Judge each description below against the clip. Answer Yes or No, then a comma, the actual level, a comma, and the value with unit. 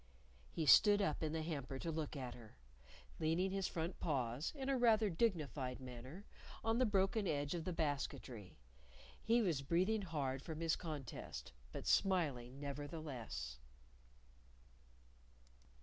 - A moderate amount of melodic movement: No, wide, 5.9 semitones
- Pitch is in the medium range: Yes, medium, 155 Hz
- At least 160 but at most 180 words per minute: No, slow, 135 wpm